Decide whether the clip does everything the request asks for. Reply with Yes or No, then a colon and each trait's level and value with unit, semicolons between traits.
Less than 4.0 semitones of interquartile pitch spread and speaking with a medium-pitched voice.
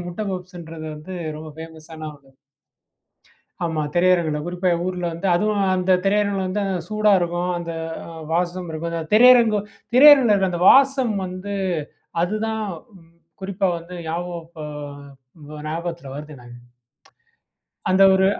Yes: average, 3.5 semitones; medium, 180 Hz